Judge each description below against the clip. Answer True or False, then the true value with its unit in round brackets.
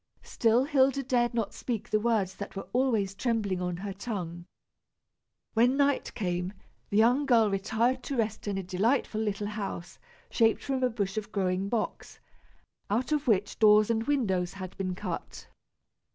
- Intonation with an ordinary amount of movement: True (3.8 semitones)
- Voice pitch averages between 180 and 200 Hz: False (215 Hz)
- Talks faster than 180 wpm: False (165 wpm)